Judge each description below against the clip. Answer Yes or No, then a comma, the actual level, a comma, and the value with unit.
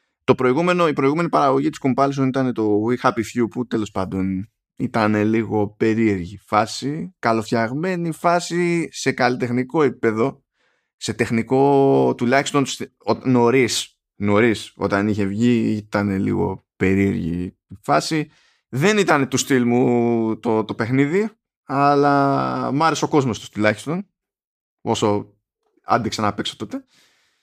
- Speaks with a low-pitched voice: Yes, low, 120 Hz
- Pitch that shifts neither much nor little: Yes, average, 4.8 semitones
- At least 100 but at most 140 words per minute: Yes, average, 120 wpm